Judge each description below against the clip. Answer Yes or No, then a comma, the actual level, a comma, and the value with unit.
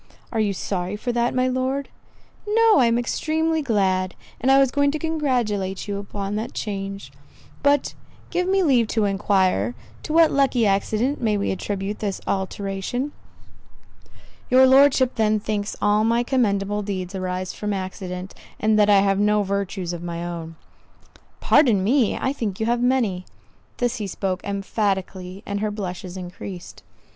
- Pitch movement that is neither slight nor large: Yes, average, 4.6 semitones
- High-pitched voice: Yes, high, 210 Hz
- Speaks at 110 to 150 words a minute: No, average, 160 wpm